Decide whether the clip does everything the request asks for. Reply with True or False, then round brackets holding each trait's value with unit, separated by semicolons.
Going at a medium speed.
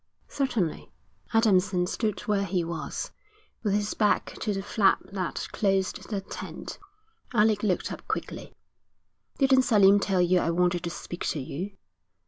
True (145 wpm)